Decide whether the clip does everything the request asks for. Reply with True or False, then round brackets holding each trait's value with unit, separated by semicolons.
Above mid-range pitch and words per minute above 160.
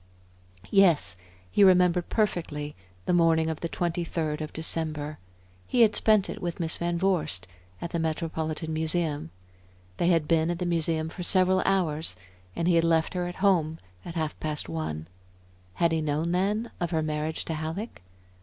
False (165 Hz; 175 wpm)